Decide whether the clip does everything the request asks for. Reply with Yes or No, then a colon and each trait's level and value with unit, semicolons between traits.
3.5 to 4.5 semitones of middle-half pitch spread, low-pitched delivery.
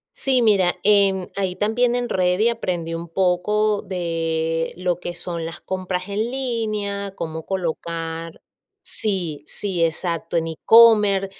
No: average, 3.9 semitones; medium, 185 Hz